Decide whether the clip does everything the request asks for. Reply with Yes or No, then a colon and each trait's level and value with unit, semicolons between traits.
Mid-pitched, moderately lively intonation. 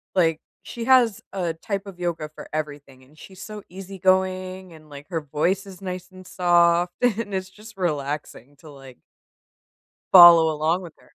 Yes: medium, 175 Hz; average, 3.5 semitones